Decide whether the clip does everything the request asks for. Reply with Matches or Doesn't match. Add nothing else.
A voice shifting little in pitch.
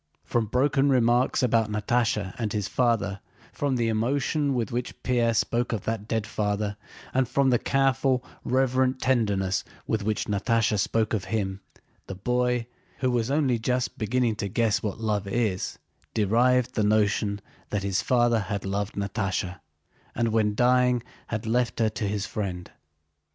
Doesn't match